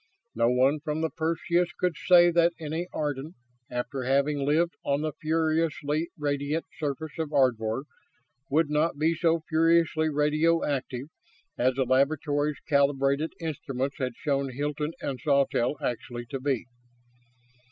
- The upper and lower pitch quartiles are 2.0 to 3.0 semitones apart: Yes, average, 2.7 semitones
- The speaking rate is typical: No, slow, 130 wpm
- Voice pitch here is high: No, medium, 150 Hz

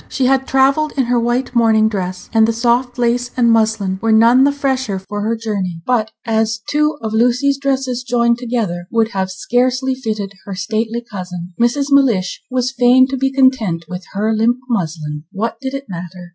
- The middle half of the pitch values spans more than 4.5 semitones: No, average, 4.1 semitones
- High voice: Yes, high, 230 Hz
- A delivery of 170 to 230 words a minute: Yes, average, 185 wpm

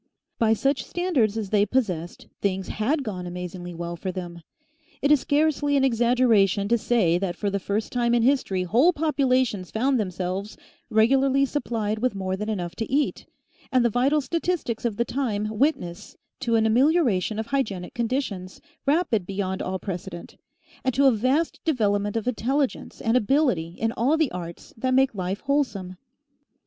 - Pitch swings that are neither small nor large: No, wide, 5.8 semitones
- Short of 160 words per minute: No, average, 165 wpm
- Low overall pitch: No, high, 225 Hz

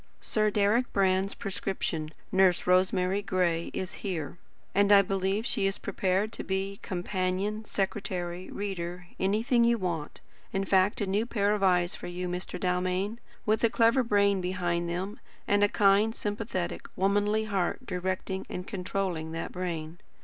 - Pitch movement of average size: No, narrow, 2.2 semitones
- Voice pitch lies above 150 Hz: Yes, high, 190 Hz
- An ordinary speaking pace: Yes, average, 150 wpm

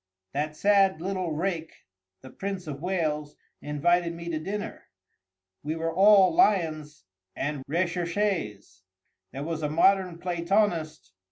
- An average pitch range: Yes, average, 3.6 semitones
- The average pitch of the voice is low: No, medium, 170 Hz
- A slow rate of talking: Yes, slow, 120 wpm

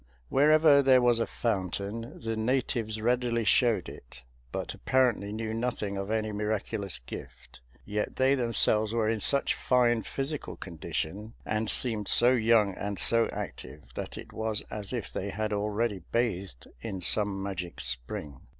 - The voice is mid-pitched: No, low, 110 Hz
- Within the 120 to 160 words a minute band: Yes, average, 150 wpm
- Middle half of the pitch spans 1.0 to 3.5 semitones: Yes, average, 3.0 semitones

